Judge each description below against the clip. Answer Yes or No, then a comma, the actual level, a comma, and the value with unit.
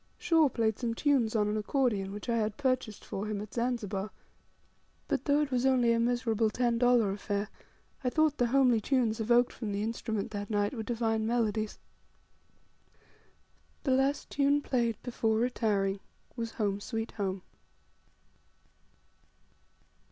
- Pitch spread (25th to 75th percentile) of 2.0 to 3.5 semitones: Yes, average, 2.9 semitones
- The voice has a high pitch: Yes, high, 230 Hz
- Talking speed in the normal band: Yes, average, 145 wpm